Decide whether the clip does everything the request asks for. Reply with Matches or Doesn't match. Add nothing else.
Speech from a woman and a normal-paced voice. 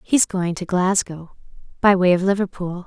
Matches